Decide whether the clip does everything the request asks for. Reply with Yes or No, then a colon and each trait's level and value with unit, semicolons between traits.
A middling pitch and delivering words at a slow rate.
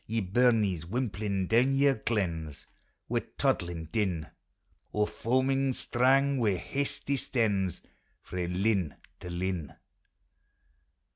No: low, 105 Hz; slow, 100 wpm